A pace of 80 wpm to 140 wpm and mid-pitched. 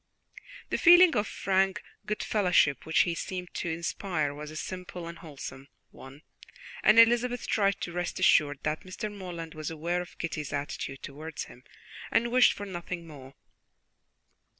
No: average, 150 wpm; medium, 175 Hz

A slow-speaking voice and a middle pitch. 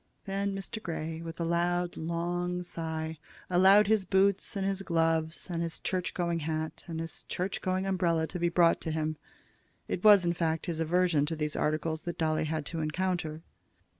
No: average, 185 wpm; medium, 170 Hz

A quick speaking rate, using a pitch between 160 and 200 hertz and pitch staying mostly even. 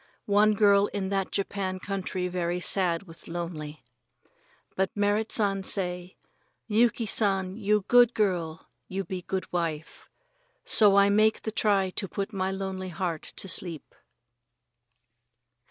No: slow, 135 wpm; high, 190 Hz; narrow, 2.3 semitones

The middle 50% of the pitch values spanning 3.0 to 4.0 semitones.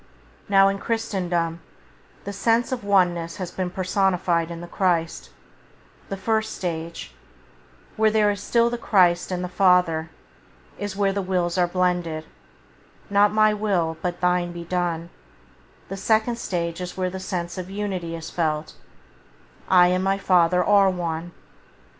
No: narrow, 2.5 semitones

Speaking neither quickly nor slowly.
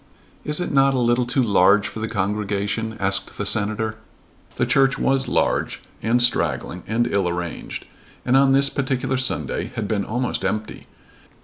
Yes: average, 165 wpm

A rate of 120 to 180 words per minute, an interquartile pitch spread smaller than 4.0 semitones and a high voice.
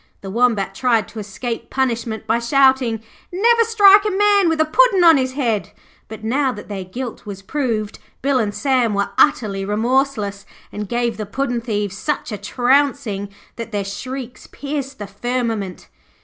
No: average, 165 wpm; average, 4.8 semitones; high, 240 Hz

